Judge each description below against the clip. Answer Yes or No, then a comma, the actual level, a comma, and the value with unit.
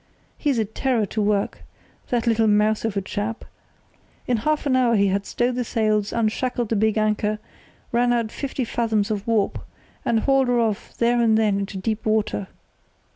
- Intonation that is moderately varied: No, narrow, 2.3 semitones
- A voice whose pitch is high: Yes, high, 220 Hz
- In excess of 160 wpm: Yes, average, 180 wpm